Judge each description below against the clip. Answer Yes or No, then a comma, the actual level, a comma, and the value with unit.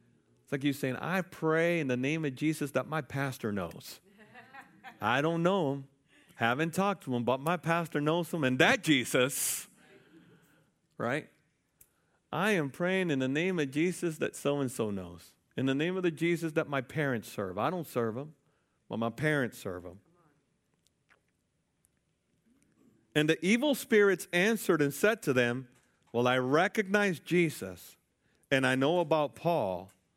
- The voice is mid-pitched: Yes, medium, 145 Hz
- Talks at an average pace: Yes, average, 160 wpm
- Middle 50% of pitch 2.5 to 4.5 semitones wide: No, average, 5.1 semitones